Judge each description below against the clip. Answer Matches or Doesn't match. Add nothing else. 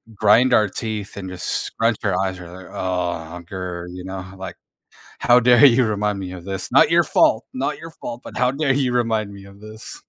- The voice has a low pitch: Matches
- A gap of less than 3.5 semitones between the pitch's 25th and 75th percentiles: Doesn't match